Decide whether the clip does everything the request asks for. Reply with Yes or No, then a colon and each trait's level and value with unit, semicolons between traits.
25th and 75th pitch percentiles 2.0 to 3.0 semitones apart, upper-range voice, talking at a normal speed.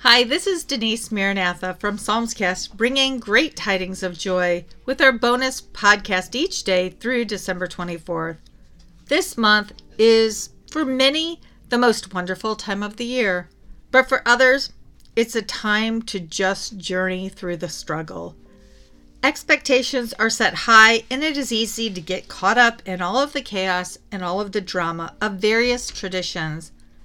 No: average, 4.9 semitones; high, 210 Hz; average, 155 wpm